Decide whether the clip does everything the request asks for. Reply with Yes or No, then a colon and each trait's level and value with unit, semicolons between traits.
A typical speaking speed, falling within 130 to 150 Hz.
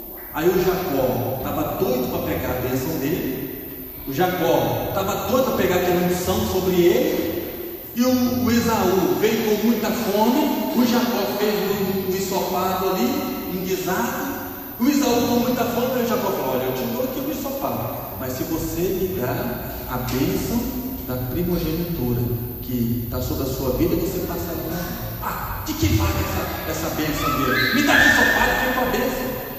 No: average, 170 wpm; medium, 185 Hz